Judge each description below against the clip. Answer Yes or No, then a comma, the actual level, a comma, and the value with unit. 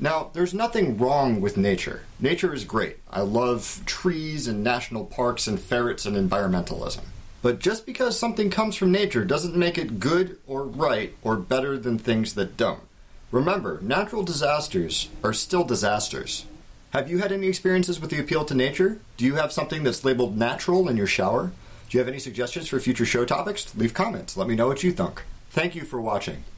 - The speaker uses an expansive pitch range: Yes, wide, 7.3 semitones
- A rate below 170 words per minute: No, average, 190 wpm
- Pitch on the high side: No, low, 135 Hz